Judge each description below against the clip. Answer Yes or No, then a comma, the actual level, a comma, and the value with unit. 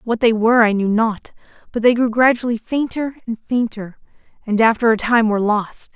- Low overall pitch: No, high, 225 Hz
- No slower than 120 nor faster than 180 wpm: No, average, 190 wpm